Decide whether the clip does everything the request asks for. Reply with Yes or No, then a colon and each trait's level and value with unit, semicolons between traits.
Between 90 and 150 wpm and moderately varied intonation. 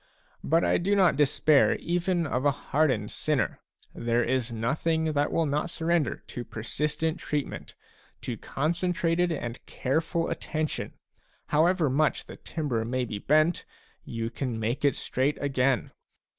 Yes: average, 140 wpm; average, 4.5 semitones